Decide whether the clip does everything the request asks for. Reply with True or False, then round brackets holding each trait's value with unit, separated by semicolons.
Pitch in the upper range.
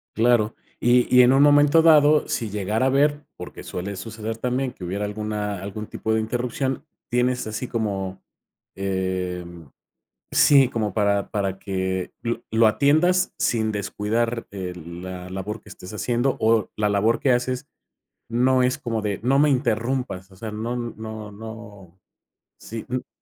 False (110 Hz)